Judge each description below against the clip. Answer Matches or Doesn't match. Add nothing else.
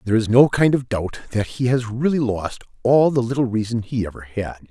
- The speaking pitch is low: Matches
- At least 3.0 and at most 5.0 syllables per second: Doesn't match